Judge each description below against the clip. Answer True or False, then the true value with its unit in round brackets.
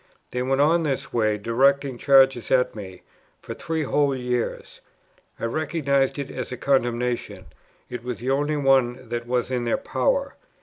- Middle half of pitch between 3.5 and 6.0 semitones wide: False (2.5 semitones)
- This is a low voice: True (130 Hz)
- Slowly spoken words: False (170 wpm)